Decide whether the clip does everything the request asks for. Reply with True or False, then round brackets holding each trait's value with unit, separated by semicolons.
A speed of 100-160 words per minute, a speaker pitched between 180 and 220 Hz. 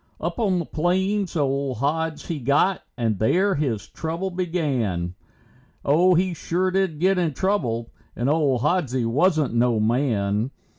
False (145 wpm; 150 Hz)